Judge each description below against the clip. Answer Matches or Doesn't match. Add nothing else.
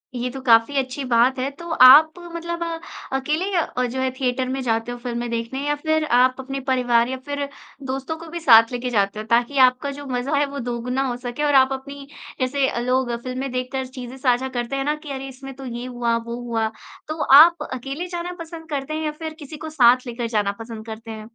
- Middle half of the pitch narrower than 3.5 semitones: Matches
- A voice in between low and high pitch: Doesn't match